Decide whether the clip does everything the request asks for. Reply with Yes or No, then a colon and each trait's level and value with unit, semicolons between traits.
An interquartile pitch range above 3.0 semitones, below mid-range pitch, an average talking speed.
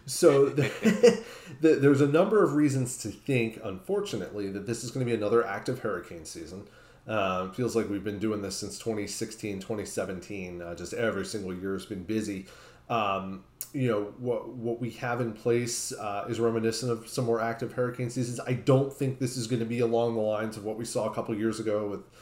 No: average, 3.4 semitones; low, 115 Hz; fast, 210 wpm